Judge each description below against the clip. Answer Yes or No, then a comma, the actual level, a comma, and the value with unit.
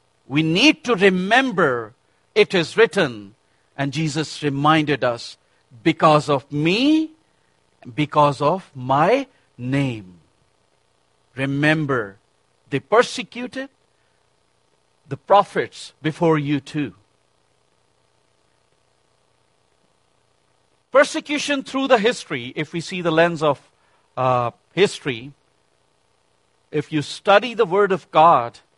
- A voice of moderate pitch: Yes, medium, 150 Hz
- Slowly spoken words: Yes, slow, 95 wpm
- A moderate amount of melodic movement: No, wide, 7.4 semitones